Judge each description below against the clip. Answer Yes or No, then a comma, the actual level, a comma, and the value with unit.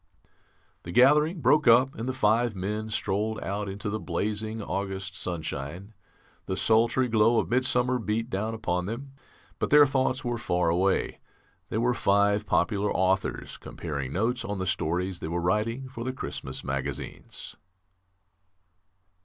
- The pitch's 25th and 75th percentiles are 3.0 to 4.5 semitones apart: Yes, average, 4.2 semitones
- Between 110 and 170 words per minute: Yes, average, 150 wpm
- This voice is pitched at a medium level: No, low, 105 Hz